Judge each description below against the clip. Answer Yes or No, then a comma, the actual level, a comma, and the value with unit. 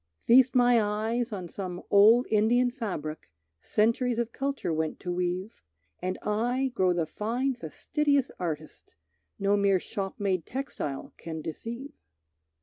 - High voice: Yes, high, 210 Hz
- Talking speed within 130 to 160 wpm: Yes, slow, 135 wpm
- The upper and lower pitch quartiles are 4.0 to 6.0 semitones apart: Yes, average, 5.3 semitones